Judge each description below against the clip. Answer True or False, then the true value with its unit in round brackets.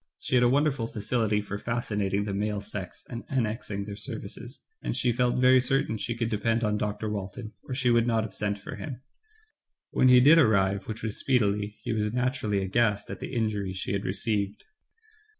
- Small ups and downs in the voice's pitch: False (3.0 semitones)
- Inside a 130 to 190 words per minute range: False (200 wpm)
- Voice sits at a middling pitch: False (110 Hz)